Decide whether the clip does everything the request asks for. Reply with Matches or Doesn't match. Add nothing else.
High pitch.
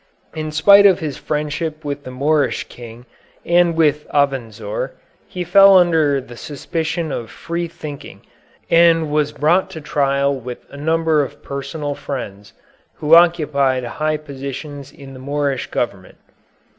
Doesn't match